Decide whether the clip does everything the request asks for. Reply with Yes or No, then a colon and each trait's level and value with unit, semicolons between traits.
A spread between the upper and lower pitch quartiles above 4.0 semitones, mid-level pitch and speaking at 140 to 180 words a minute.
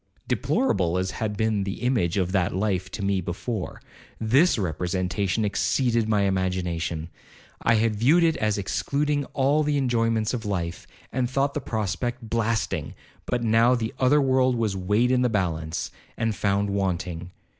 No: average, 4.8 semitones; low, 110 Hz; average, 155 wpm